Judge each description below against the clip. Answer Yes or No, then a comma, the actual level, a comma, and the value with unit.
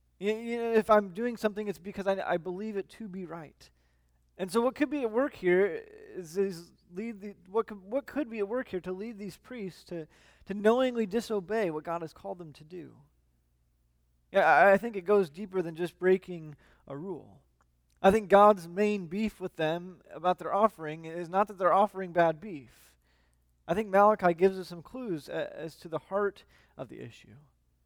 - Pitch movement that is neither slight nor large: Yes, average, 4.6 semitones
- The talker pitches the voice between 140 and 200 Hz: Yes, high, 190 Hz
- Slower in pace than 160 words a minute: No, average, 200 wpm